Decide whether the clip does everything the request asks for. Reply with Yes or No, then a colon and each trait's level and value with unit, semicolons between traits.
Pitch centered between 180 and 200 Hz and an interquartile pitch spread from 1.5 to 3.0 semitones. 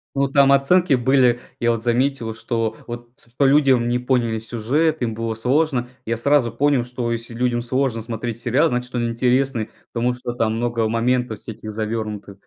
No: low, 120 Hz; narrow, 2.4 semitones